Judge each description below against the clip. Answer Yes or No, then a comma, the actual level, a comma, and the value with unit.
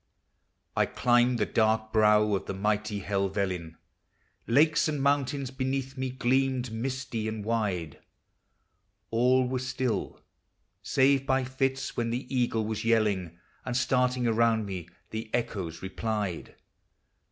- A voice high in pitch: No, low, 115 Hz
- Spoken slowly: Yes, slow, 130 wpm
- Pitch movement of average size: Yes, average, 3.6 semitones